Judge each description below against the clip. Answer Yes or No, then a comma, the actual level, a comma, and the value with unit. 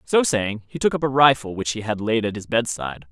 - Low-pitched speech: Yes, low, 115 Hz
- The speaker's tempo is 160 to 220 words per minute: No, fast, 270 wpm